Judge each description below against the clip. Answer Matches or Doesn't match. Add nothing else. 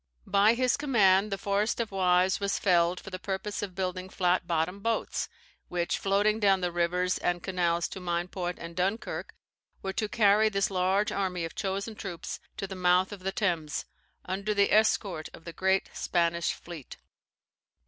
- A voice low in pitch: Doesn't match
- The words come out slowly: Doesn't match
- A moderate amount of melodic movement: Doesn't match